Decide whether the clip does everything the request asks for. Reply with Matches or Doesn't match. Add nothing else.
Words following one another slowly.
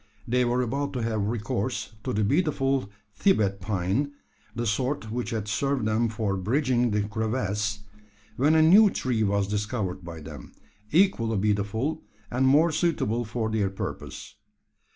Doesn't match